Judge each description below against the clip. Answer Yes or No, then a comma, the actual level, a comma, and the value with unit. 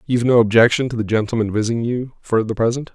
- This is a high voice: No, low, 115 Hz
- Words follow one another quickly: Yes, fast, 225 wpm